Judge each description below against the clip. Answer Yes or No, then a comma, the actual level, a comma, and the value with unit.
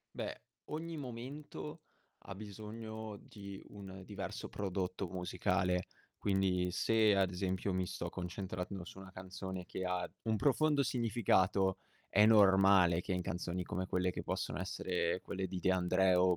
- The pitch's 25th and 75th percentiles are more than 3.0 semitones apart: No, narrow, 2.4 semitones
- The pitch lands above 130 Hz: No, very low, 95 Hz